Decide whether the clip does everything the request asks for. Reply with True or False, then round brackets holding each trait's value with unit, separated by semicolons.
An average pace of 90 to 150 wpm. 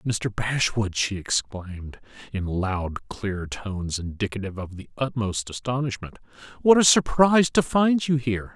True (140 wpm)